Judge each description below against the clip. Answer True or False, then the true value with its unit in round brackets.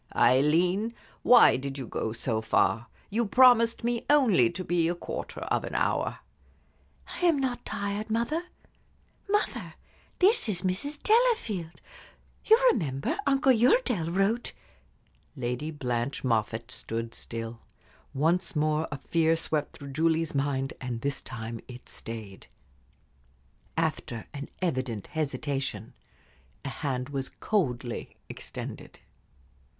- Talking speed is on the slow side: True (125 wpm)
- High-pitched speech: False (155 Hz)